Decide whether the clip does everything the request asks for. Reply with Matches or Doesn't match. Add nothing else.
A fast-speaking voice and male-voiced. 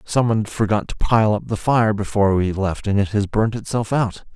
Matches